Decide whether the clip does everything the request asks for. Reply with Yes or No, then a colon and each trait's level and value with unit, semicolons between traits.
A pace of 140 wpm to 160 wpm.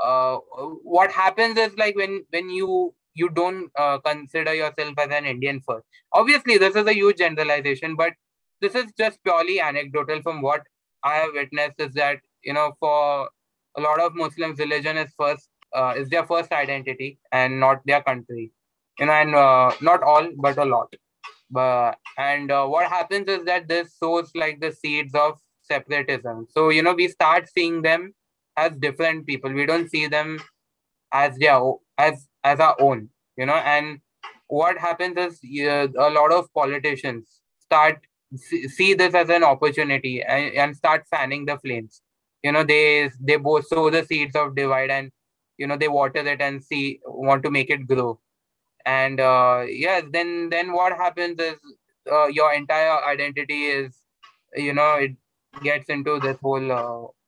No: average, 175 wpm